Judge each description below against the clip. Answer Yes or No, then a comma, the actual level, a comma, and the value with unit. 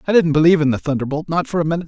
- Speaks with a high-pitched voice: No, medium, 160 Hz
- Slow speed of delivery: No, fast, 320 wpm